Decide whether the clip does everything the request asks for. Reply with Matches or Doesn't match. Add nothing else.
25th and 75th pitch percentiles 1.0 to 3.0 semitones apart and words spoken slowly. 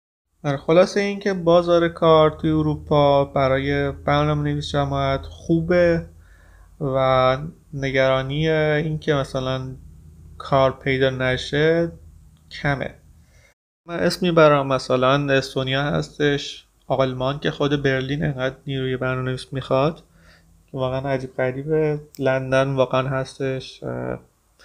Matches